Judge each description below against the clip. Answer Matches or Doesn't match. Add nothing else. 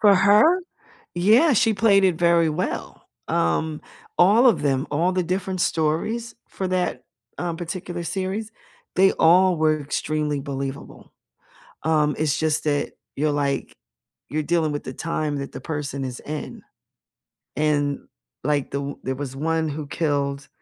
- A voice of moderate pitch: Matches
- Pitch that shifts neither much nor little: Matches